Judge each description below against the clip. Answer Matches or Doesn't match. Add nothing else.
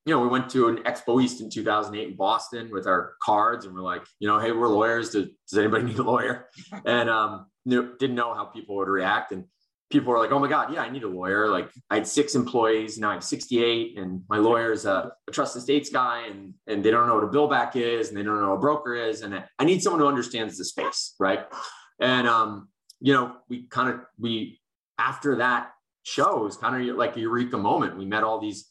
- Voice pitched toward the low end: Matches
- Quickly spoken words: Matches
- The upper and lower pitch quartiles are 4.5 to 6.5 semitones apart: Doesn't match